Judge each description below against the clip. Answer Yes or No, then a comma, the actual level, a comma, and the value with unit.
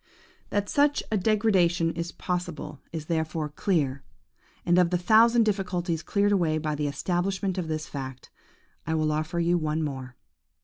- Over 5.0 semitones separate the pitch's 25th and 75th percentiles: No, average, 3.7 semitones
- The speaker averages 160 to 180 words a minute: Yes, average, 165 wpm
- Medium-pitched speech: Yes, medium, 170 Hz